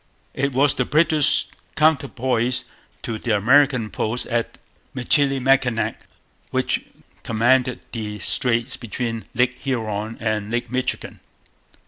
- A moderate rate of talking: No, slow, 105 wpm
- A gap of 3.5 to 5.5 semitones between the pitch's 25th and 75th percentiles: No, average, 3.0 semitones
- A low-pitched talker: Yes, low, 125 Hz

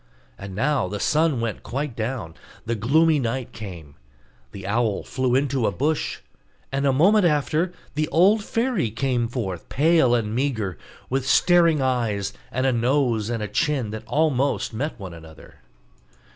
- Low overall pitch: Yes, low, 130 Hz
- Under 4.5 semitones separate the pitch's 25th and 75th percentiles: No, wide, 5.4 semitones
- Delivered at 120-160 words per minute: Yes, average, 155 wpm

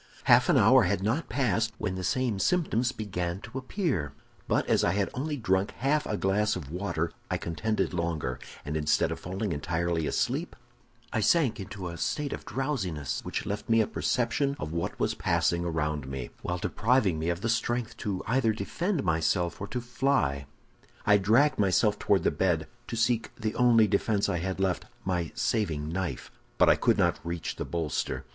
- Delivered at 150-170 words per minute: No, average, 185 wpm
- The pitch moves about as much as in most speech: No, wide, 5.7 semitones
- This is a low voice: Yes, low, 100 Hz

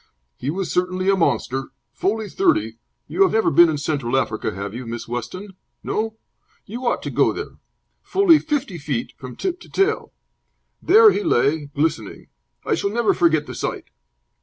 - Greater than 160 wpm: Yes, average, 170 wpm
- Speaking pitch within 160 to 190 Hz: Yes, medium, 185 Hz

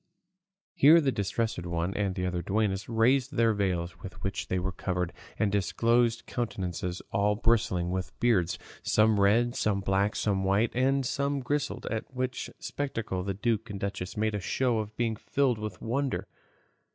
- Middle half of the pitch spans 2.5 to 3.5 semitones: No, average, 3.9 semitones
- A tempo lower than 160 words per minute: No, average, 165 wpm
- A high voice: No, low, 105 Hz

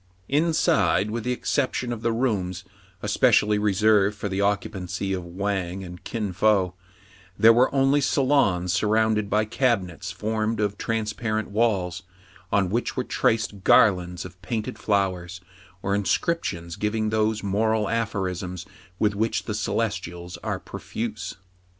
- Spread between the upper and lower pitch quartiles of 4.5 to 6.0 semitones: No, average, 3.0 semitones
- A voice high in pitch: No, low, 105 Hz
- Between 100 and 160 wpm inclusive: Yes, average, 140 wpm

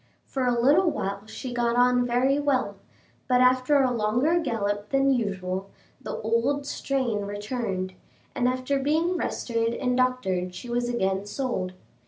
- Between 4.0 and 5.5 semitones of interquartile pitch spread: Yes, average, 4.3 semitones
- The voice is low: No, high, 245 Hz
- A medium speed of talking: Yes, average, 150 wpm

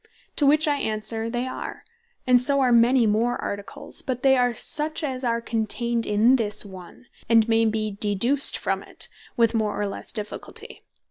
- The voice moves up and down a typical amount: Yes, average, 3.0 semitones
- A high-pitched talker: Yes, high, 230 Hz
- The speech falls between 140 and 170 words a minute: No, average, 180 wpm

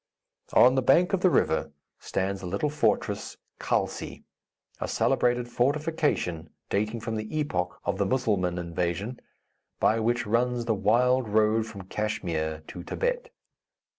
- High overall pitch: No, low, 110 Hz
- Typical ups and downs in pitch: Yes, average, 4.8 semitones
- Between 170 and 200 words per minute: No, slow, 135 wpm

